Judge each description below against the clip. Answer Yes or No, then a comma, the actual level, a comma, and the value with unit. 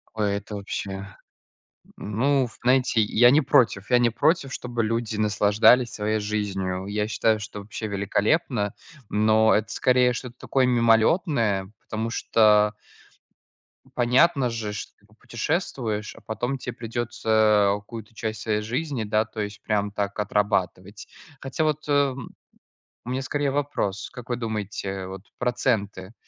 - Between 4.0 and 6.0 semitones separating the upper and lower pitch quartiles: No, average, 3.1 semitones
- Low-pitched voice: Yes, low, 110 Hz